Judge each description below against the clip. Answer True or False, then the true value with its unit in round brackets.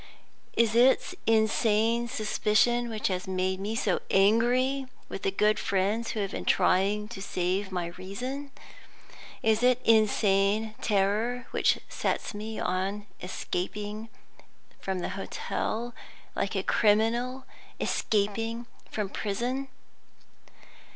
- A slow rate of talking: True (115 wpm)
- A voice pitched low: False (215 Hz)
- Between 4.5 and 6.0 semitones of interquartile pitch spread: False (3.0 semitones)